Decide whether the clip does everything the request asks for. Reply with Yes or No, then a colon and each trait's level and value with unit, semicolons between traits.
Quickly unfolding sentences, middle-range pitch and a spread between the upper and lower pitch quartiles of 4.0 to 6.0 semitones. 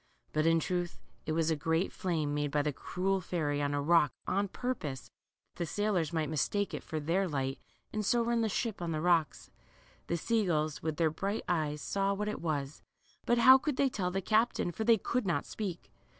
Yes: fast, 220 wpm; medium, 175 Hz; average, 4.8 semitones